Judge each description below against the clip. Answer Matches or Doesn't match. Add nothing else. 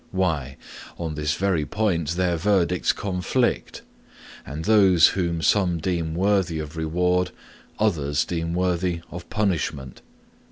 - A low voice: Matches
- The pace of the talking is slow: Matches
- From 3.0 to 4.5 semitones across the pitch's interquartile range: Doesn't match